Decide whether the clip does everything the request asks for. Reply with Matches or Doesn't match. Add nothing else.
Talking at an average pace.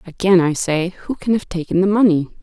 Doesn't match